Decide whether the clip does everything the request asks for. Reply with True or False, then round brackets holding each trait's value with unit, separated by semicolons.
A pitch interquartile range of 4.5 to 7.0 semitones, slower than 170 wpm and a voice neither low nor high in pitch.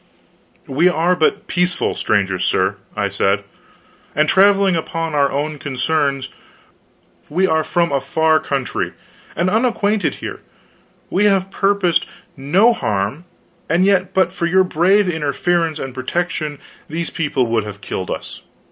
True (5.1 semitones; 140 wpm; 160 Hz)